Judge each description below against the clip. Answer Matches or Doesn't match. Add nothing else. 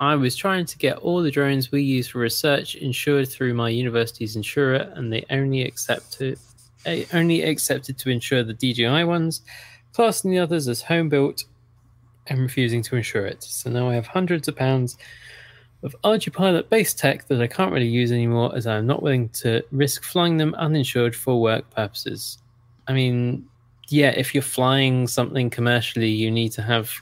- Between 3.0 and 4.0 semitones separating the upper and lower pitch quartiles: Matches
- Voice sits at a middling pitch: Doesn't match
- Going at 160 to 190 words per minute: Matches